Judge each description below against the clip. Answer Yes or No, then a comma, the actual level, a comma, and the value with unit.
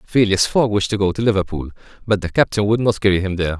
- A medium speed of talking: No, fast, 250 wpm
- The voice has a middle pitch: No, low, 100 Hz